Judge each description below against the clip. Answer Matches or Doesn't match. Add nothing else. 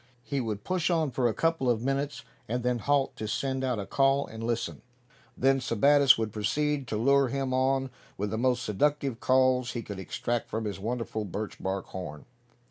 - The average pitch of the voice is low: Matches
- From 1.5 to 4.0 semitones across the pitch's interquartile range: Matches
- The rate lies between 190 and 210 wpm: Matches